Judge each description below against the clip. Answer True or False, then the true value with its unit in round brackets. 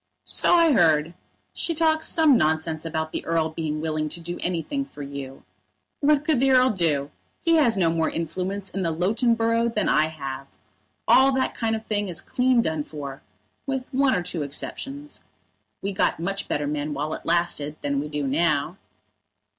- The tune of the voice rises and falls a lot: True (7.7 semitones)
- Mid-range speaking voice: True (170 Hz)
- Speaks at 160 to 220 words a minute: True (185 wpm)